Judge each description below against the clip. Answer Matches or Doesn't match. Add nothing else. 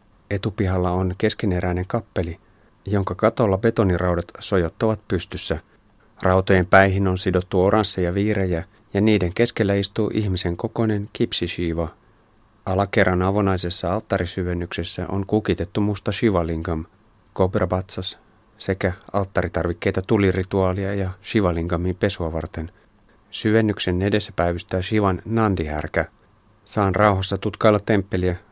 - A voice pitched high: Doesn't match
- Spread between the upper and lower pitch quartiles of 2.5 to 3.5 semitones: Matches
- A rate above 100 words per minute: Doesn't match